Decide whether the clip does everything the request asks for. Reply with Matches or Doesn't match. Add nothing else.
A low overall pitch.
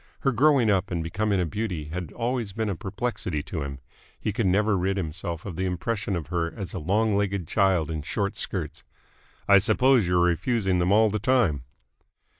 Matches